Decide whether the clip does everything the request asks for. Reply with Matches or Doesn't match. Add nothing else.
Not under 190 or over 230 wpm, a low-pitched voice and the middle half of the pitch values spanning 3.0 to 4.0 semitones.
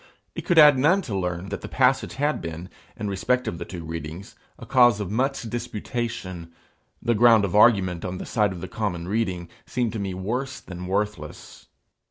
Doesn't match